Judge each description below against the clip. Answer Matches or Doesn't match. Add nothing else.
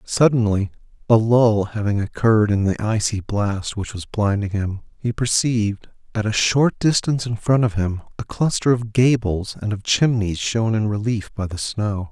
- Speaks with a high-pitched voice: Doesn't match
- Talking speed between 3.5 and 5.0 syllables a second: Matches